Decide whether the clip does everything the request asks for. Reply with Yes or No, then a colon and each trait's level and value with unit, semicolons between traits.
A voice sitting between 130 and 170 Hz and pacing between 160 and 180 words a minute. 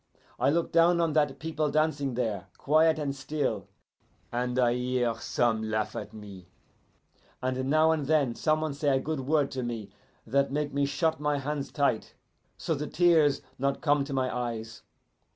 Yes: medium, 140 Hz; average, 175 wpm